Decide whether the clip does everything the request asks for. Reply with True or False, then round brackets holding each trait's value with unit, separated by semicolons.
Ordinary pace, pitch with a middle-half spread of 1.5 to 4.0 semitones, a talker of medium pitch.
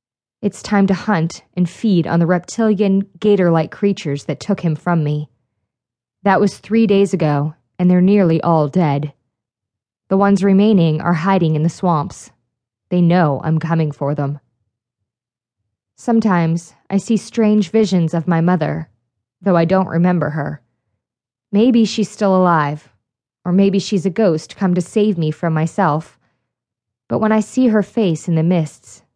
False (160 wpm; 5.5 semitones; 170 Hz)